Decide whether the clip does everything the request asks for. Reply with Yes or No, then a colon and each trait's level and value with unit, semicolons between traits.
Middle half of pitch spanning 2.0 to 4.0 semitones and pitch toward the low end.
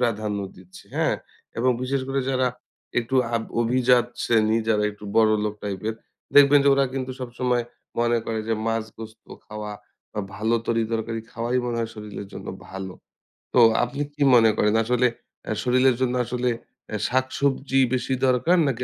Yes: average, 2.7 semitones; low, 120 Hz